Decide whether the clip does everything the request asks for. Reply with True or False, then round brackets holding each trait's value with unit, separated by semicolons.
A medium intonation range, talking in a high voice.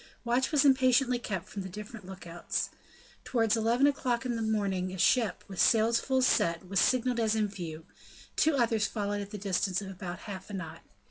True (4.2 semitones; 215 Hz)